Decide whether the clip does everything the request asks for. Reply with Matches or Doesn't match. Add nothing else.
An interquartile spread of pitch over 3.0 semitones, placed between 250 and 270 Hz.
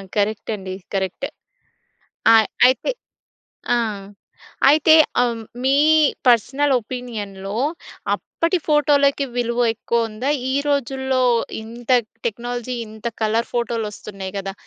Doesn't match